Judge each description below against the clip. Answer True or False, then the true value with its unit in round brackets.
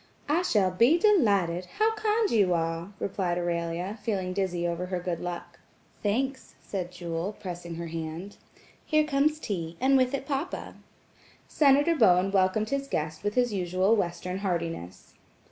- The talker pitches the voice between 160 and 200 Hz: True (190 Hz)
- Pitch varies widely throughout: True (7.2 semitones)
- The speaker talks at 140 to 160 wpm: True (150 wpm)